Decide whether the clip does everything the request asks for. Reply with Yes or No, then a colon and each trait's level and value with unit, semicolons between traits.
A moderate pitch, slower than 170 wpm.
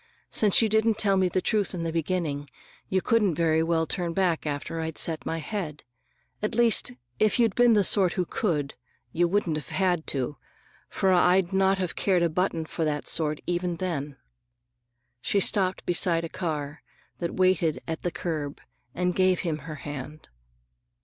No: medium, 175 Hz; average, 175 wpm